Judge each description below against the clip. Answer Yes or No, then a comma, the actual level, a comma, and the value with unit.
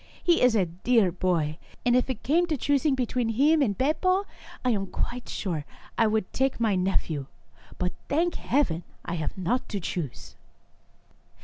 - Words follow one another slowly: No, average, 175 wpm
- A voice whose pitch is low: No, high, 225 Hz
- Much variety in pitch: Yes, wide, 6.8 semitones